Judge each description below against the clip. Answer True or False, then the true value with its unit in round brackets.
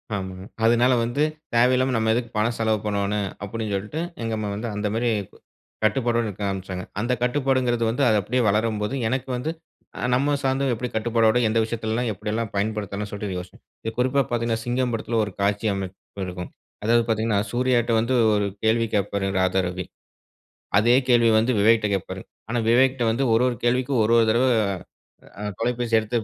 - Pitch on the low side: True (115 Hz)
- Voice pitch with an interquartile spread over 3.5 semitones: False (2.8 semitones)